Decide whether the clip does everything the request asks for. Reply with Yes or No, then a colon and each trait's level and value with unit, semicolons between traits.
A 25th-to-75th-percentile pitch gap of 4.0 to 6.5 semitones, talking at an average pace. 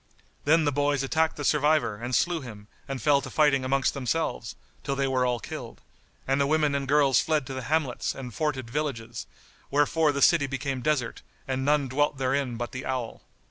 No: narrow, 2.4 semitones; average, 195 wpm